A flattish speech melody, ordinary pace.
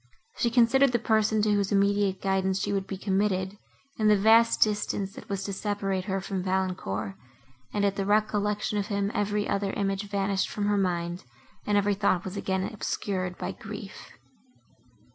Yes: narrow, 1.5 semitones; average, 175 wpm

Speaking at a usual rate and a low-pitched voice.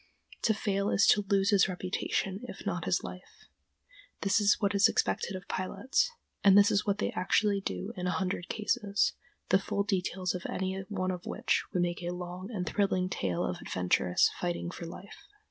No: average, 190 wpm; high, 190 Hz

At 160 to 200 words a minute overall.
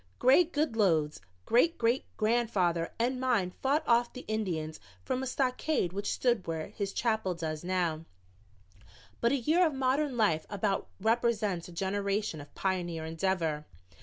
No: average, 145 wpm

